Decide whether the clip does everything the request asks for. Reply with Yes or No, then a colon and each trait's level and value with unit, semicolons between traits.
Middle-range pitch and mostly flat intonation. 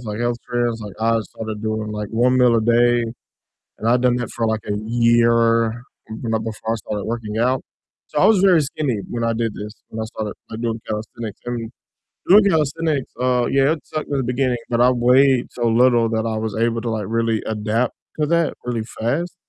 No: low, 115 Hz; narrow, 2.1 semitones